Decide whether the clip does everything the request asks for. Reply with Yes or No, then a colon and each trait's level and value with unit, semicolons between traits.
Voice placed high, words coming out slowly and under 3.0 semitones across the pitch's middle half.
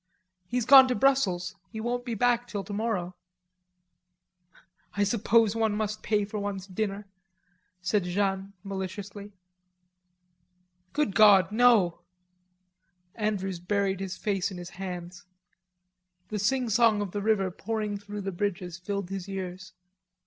Yes: high, 205 Hz; slow, 125 wpm; narrow, 2.4 semitones